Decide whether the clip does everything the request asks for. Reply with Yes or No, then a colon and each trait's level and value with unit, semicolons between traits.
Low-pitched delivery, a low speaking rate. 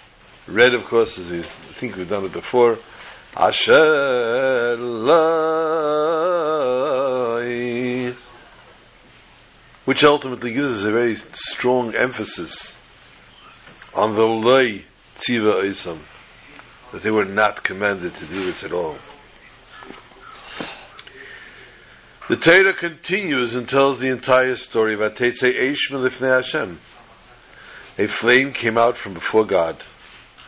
Yes: low, 125 Hz; slow, 105 wpm